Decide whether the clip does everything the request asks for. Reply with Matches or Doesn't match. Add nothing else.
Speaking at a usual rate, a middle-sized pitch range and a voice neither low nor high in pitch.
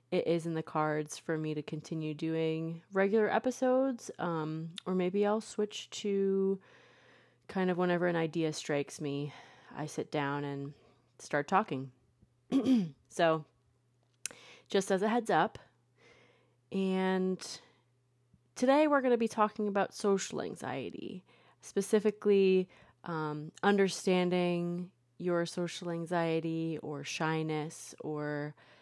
Doesn't match